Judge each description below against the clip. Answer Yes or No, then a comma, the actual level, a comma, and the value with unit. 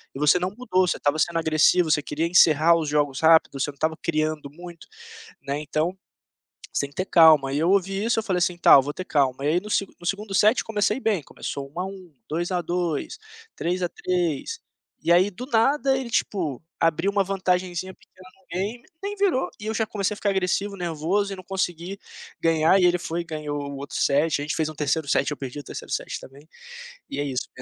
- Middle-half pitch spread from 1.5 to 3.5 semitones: No, average, 4.3 semitones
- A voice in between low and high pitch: Yes, medium, 175 Hz